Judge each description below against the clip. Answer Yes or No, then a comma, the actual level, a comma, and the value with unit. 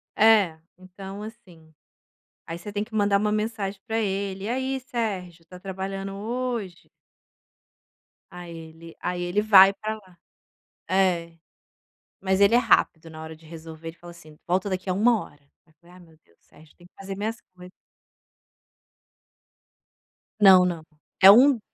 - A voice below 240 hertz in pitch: Yes, high, 190 Hz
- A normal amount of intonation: Yes, average, 3.6 semitones